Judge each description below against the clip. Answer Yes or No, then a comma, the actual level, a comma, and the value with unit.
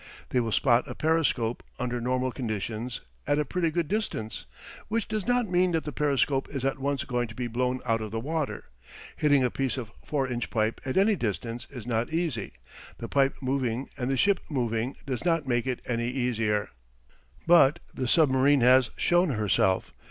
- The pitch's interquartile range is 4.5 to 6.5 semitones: No, average, 4.0 semitones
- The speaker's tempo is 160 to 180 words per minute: No, average, 190 wpm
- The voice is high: No, low, 130 Hz